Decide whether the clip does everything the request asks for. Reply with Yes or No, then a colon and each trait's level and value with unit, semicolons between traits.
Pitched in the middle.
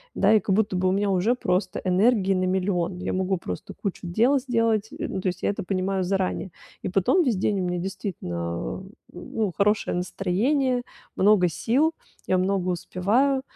No: high, 195 Hz